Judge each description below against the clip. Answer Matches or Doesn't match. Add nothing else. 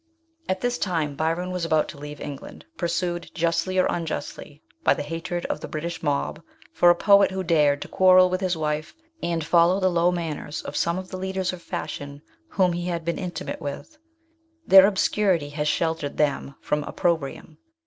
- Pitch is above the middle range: Doesn't match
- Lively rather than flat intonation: Doesn't match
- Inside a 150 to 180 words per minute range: Doesn't match